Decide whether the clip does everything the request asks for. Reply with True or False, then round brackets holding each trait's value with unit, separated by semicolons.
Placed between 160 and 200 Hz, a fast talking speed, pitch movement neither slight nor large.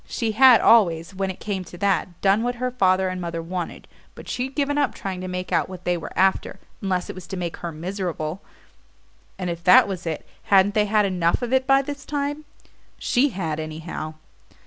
True (190 Hz; 210 wpm; 4.8 semitones)